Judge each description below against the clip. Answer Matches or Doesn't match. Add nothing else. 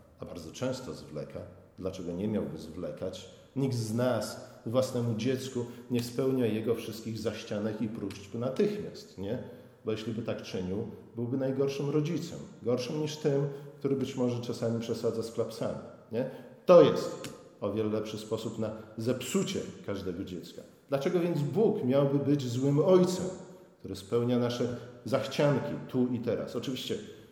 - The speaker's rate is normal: Matches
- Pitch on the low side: Matches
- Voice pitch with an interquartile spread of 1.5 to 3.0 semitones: Doesn't match